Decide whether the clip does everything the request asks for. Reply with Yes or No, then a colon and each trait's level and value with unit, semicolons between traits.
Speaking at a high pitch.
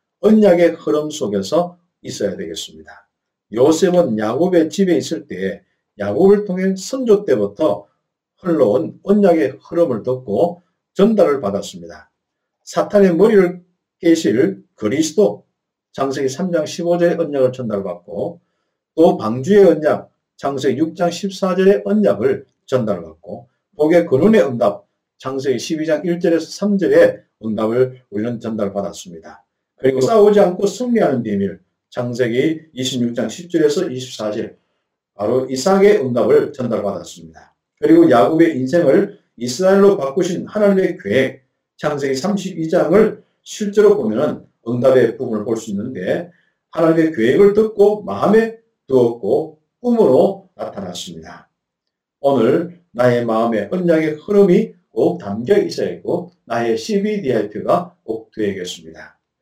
No: medium, 165 Hz